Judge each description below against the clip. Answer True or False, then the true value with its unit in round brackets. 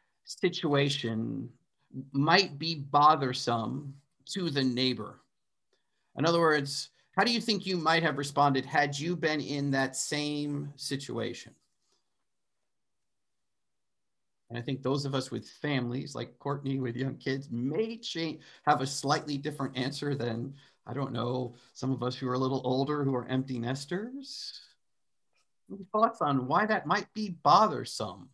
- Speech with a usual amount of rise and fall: True (3.2 semitones)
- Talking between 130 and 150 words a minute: True (145 wpm)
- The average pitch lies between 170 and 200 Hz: False (140 Hz)